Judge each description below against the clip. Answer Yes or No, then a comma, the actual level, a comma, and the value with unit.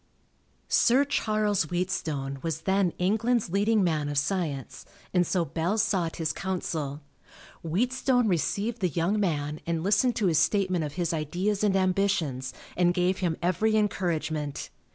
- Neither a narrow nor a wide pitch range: Yes, average, 4.3 semitones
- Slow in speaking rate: No, average, 145 wpm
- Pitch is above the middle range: No, medium, 180 Hz